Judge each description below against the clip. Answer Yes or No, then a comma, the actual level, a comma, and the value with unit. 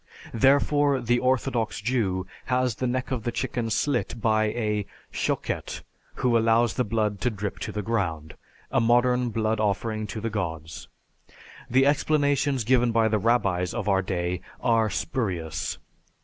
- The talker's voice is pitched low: Yes, low, 115 Hz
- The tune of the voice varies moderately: Yes, average, 3.4 semitones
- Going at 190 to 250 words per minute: No, average, 150 wpm